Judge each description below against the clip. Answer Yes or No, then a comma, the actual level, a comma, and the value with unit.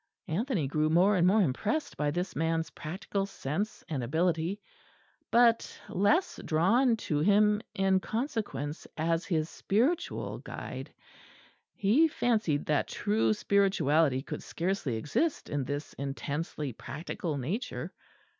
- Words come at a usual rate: No, slow, 120 wpm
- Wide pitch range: Yes, wide, 5.9 semitones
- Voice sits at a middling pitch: Yes, medium, 170 Hz